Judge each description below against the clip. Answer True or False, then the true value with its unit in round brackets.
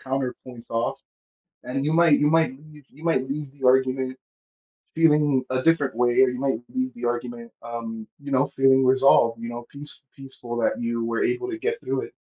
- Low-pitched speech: True (130 Hz)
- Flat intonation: False (3.7 semitones)